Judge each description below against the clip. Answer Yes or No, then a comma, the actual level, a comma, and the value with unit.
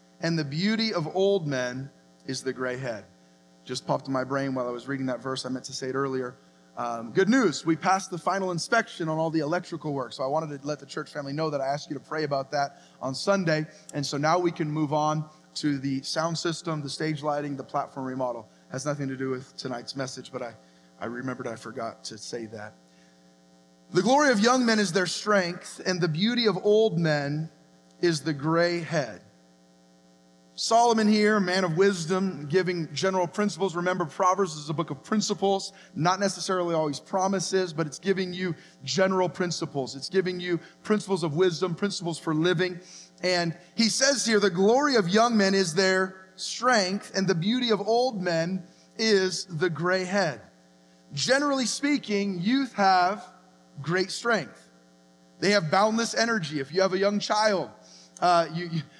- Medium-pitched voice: Yes, medium, 170 Hz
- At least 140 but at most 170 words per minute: No, average, 190 wpm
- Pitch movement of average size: No, wide, 6.1 semitones